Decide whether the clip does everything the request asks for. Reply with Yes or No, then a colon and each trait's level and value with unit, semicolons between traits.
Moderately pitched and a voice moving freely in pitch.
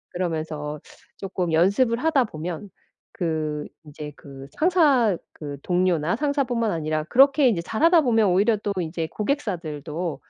Yes: medium, 180 Hz; wide, 7.2 semitones